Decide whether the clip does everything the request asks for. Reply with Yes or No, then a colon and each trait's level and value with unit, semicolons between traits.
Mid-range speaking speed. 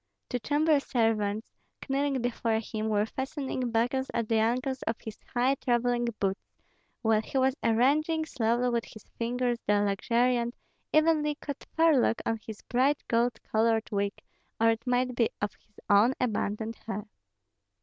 Yes: average, 150 wpm